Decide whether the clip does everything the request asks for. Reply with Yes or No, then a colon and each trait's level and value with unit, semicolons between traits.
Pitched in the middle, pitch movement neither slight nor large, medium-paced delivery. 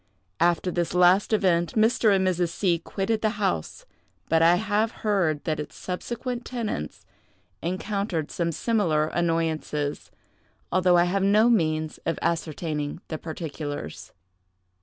No: medium, 175 Hz; average, 4.4 semitones; slow, 130 wpm